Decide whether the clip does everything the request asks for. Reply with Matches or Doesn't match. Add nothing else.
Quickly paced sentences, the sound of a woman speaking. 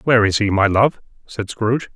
Doesn't match